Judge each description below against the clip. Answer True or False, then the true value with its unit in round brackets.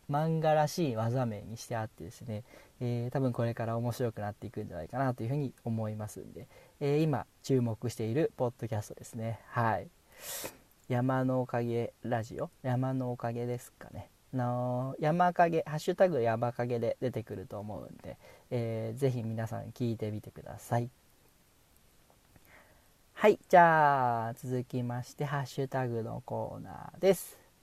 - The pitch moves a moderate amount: True (3.2 semitones)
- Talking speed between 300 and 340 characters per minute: True (325 characters per minute)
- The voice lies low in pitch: True (120 Hz)